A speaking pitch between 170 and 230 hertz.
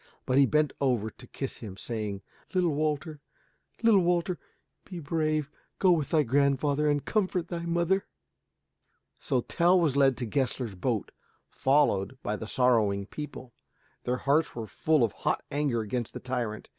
No: medium, 140 Hz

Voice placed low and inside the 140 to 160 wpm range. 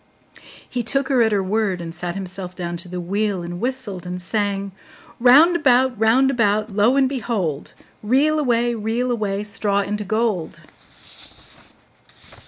No: high, 210 Hz; average, 150 wpm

